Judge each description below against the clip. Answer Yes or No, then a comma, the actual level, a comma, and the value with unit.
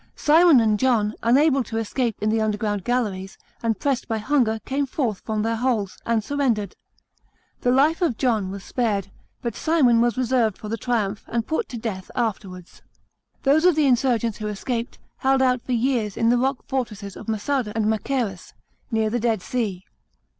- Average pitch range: Yes, average, 3.5 semitones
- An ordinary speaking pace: Yes, average, 180 wpm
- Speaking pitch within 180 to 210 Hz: No, high, 230 Hz